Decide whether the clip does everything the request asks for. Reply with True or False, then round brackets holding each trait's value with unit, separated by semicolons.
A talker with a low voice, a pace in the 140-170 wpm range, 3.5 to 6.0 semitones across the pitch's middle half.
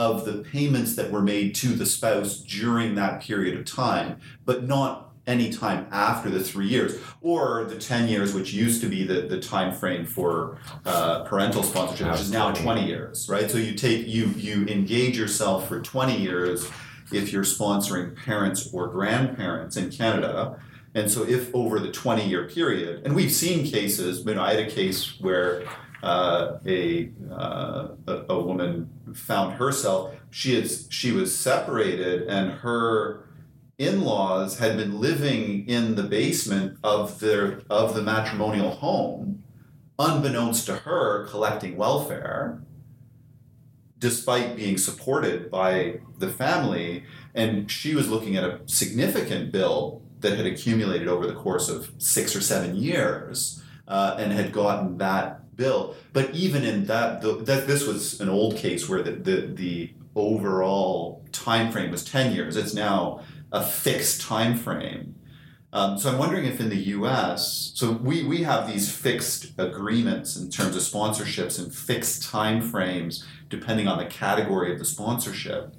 True (110 Hz; 160 wpm; 4.4 semitones)